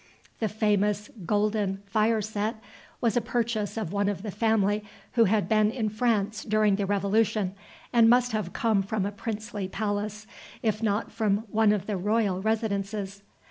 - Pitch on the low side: No, high, 210 Hz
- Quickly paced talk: No, average, 165 wpm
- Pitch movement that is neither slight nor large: No, narrow, 1.6 semitones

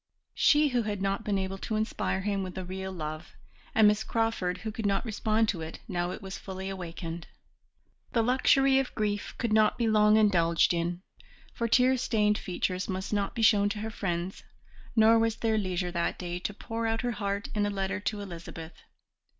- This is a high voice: Yes, high, 205 Hz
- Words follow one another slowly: No, average, 200 wpm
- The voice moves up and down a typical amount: Yes, average, 3.1 semitones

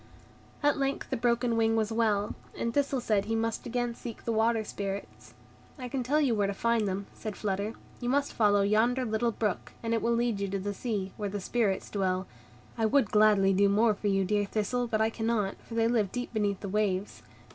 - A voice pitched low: No, high, 220 Hz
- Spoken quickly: Yes, fast, 220 wpm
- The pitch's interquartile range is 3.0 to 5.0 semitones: No, narrow, 2.6 semitones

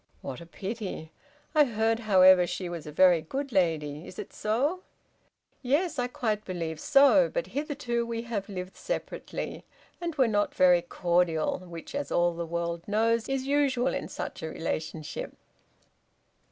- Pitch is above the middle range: Yes, high, 205 Hz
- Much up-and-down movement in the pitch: Yes, wide, 7.0 semitones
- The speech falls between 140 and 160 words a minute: Yes, average, 155 wpm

